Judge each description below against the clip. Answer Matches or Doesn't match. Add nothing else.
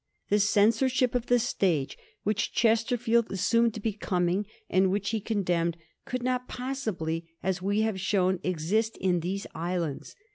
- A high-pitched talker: Matches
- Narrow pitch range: Doesn't match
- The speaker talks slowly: Doesn't match